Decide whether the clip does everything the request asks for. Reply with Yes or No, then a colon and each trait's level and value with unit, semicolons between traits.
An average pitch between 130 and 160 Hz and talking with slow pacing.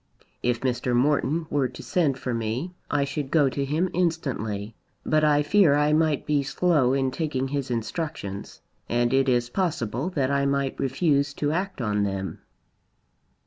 No: medium, 140 Hz; average, 165 wpm